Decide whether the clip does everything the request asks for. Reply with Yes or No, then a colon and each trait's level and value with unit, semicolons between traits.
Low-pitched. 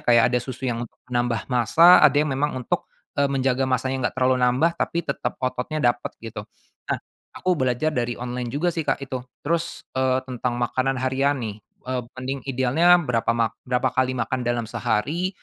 Yes: low, 130 Hz